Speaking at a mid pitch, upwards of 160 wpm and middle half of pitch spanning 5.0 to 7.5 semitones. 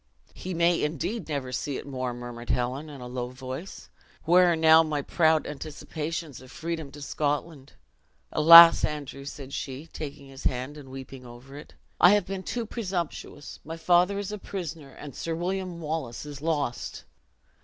No: medium, 150 Hz; average, 170 wpm; average, 4.0 semitones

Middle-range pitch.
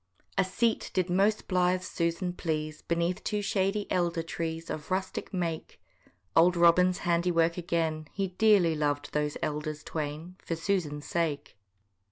Yes: medium, 170 Hz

